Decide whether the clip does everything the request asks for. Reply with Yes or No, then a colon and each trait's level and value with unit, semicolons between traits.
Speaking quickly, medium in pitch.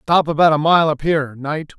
Yes: fast, 235 wpm; medium, 155 Hz